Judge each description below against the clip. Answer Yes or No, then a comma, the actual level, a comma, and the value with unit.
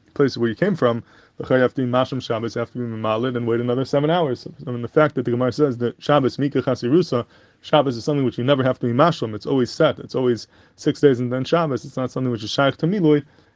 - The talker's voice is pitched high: No, low, 130 Hz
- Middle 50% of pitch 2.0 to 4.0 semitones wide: Yes, average, 3.4 semitones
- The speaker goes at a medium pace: No, fast, 265 wpm